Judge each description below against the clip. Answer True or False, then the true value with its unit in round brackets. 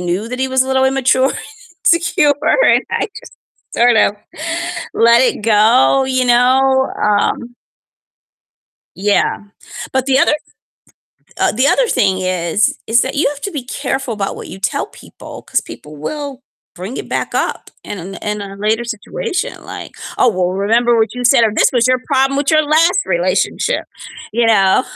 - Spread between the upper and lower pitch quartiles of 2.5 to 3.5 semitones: False (4.3 semitones)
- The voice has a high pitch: True (245 Hz)